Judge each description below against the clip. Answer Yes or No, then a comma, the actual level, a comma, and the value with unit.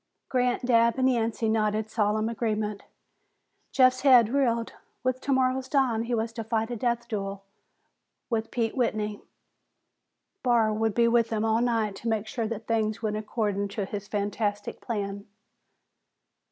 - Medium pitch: No, high, 225 Hz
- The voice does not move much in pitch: Yes, narrow, 2.1 semitones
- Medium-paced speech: Yes, average, 150 wpm